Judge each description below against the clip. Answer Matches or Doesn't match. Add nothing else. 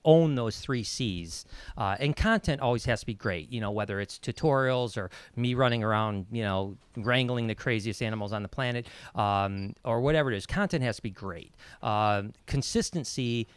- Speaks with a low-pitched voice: Matches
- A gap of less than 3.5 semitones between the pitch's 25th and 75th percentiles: Doesn't match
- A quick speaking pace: Doesn't match